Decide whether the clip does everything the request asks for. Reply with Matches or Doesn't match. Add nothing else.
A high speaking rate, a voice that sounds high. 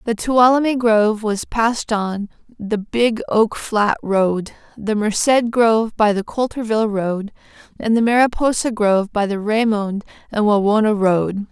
Doesn't match